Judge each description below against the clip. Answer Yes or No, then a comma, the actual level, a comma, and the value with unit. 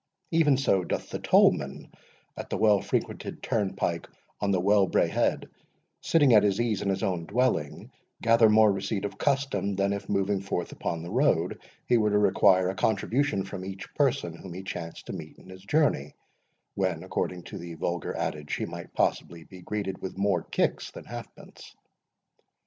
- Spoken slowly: No, average, 175 wpm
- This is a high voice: No, low, 100 Hz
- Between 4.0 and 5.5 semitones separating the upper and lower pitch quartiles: No, average, 3.2 semitones